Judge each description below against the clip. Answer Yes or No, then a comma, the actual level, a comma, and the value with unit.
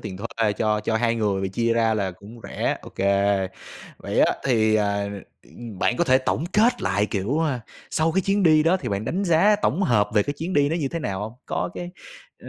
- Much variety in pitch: Yes, wide, 7.6 semitones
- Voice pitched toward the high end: No, low, 115 Hz